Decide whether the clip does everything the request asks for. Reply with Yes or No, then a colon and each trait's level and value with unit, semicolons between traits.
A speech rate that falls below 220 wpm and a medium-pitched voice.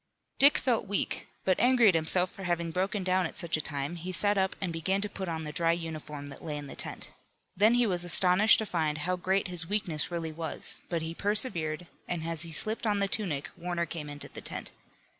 No: fast, 230 wpm; medium, 175 Hz